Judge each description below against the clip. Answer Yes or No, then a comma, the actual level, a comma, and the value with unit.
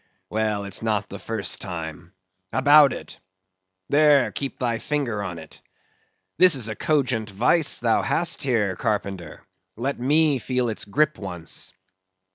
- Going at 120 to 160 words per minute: Yes, average, 140 wpm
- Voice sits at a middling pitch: No, low, 115 Hz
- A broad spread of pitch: Yes, wide, 5.8 semitones